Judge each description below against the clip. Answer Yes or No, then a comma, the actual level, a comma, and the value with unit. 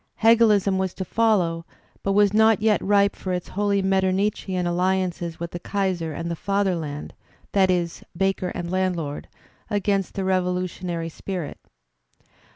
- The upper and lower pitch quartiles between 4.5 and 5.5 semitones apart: No, narrow, 2.4 semitones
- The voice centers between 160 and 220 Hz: Yes, high, 190 Hz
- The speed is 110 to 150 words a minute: Yes, average, 140 wpm